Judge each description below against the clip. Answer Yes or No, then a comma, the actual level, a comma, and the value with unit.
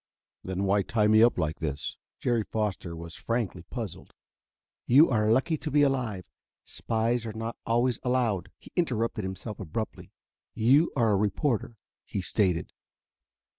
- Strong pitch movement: No, average, 3.8 semitones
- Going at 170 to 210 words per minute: No, average, 150 wpm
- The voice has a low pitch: Yes, low, 110 Hz